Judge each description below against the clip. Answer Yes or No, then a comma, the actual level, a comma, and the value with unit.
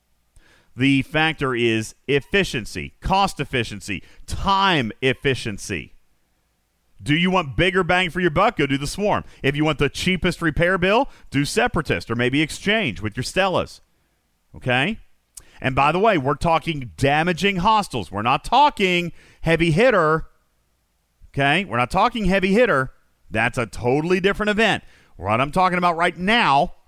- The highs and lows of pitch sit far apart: Yes, wide, 7.1 semitones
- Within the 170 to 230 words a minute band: No, average, 145 wpm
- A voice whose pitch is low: No, medium, 150 Hz